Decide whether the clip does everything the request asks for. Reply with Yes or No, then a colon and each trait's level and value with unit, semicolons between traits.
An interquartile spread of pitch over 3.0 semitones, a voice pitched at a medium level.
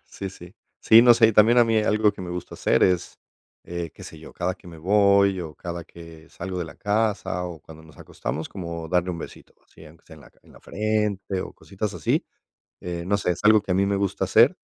No: average, 3.4 semitones; very low, 90 Hz